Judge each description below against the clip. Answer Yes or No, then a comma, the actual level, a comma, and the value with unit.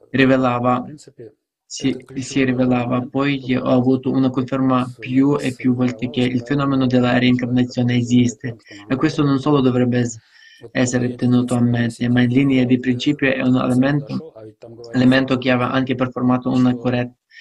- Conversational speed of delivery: Yes, average, 150 wpm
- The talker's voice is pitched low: Yes, low, 125 Hz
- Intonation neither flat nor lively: No, narrow, 1.2 semitones